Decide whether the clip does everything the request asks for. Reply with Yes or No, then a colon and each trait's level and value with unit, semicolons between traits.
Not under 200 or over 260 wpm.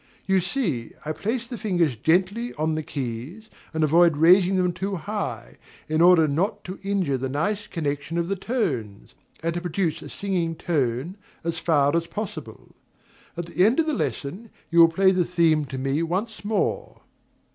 No: average, 180 wpm